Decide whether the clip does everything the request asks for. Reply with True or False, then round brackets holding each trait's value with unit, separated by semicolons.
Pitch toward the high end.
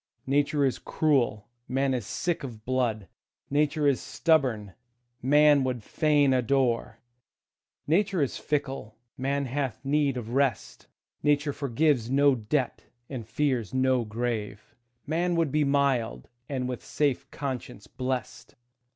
False (135 Hz)